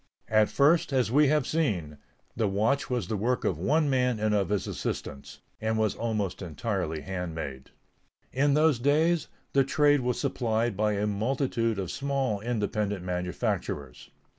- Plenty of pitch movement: Yes, wide, 5.8 semitones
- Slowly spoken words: No, average, 155 wpm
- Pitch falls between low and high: No, low, 110 Hz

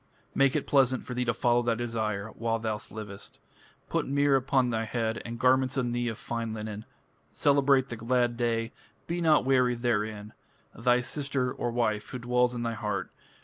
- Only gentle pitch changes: Yes, narrow, 2.2 semitones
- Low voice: Yes, low, 120 Hz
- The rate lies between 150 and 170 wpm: No, average, 180 wpm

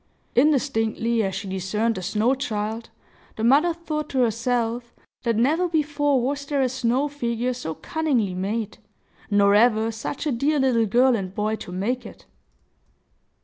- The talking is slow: No, average, 155 wpm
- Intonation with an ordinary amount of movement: Yes, average, 4.0 semitones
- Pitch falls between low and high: No, high, 235 Hz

